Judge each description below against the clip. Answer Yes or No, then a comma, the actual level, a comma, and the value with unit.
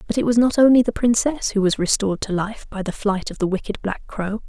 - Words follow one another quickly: Yes, fast, 270 wpm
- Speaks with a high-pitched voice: Yes, high, 210 Hz